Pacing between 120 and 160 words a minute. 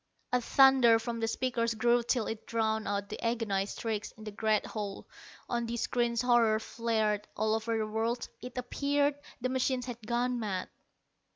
No: average, 175 wpm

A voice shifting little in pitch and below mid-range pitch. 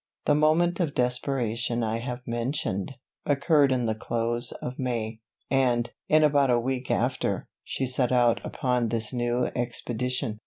Yes: narrow, 2.3 semitones; low, 125 Hz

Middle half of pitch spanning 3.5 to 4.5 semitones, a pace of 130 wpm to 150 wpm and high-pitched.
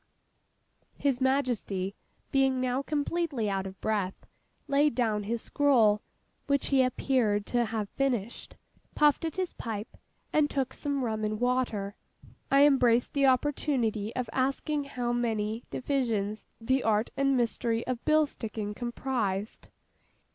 Yes: average, 4.1 semitones; slow, 135 wpm; high, 245 Hz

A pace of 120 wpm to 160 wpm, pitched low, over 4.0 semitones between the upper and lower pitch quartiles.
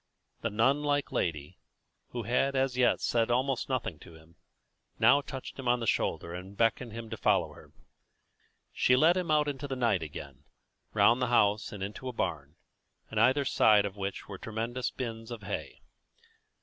No: average, 180 wpm; low, 115 Hz; average, 4.4 semitones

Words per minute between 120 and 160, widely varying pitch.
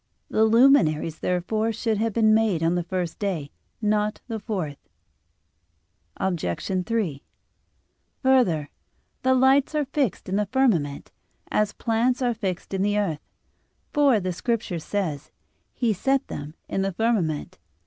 No: average, 140 wpm; average, 4.9 semitones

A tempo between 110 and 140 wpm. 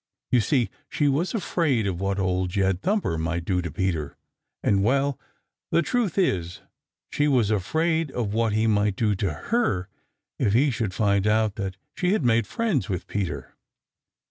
No: average, 170 wpm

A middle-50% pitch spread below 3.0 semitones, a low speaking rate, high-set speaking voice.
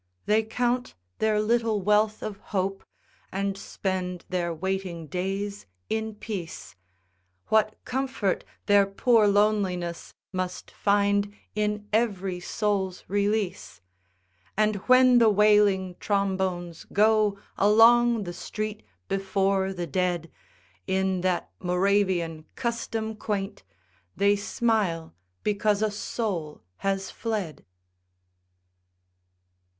Yes: narrow, 2.4 semitones; slow, 100 wpm; high, 200 Hz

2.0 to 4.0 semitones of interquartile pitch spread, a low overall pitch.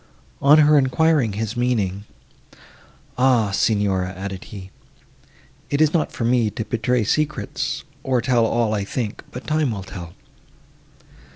No: average, 4.8 semitones; low, 115 Hz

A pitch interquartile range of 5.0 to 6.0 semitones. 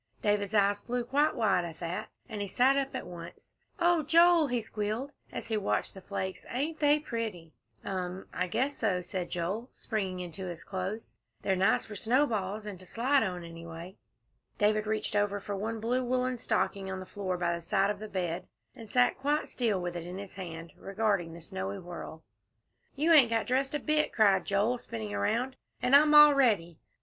Yes: wide, 5.4 semitones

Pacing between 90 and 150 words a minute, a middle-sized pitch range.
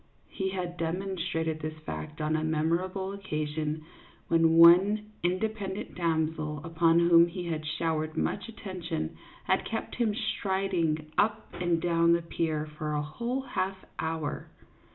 Yes: slow, 135 wpm; average, 3.4 semitones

